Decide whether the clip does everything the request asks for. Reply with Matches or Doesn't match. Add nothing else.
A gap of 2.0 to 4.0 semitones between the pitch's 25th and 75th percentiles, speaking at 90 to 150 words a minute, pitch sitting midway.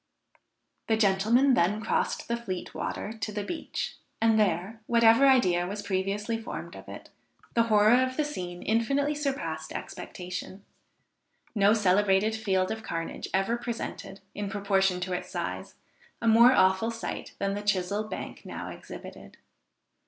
Doesn't match